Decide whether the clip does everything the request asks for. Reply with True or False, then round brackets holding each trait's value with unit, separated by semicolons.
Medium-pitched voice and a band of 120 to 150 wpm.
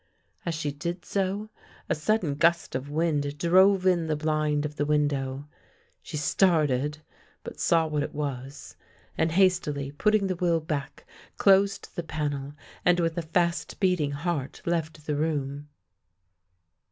True (155 Hz; 145 wpm)